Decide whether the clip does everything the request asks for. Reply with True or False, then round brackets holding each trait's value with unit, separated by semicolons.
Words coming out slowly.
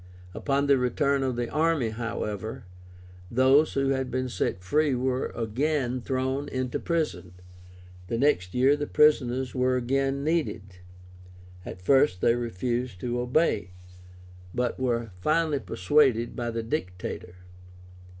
True (130 wpm)